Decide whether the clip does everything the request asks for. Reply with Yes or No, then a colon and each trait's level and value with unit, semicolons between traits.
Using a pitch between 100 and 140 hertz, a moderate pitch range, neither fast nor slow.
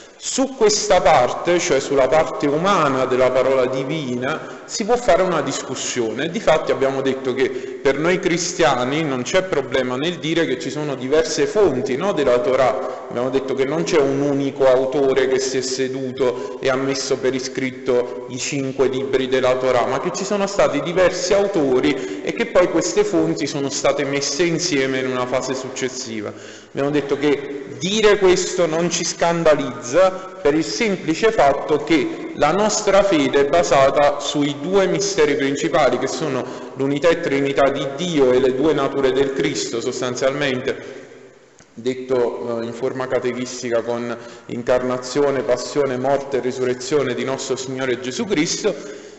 Yes: low, 135 Hz; average, 4.5 semitones; average, 155 wpm